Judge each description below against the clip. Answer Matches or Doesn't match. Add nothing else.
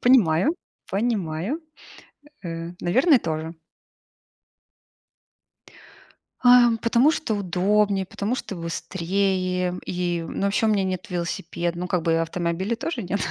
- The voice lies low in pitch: Doesn't match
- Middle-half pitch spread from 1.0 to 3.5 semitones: Doesn't match